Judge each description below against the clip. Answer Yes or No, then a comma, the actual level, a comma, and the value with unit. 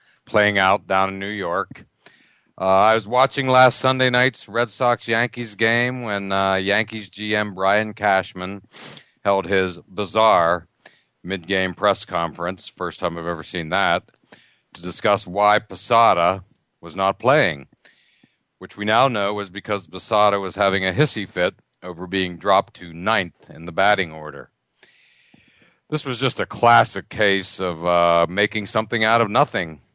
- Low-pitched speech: Yes, low, 100 Hz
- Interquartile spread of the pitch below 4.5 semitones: Yes, average, 3.1 semitones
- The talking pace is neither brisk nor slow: Yes, average, 155 wpm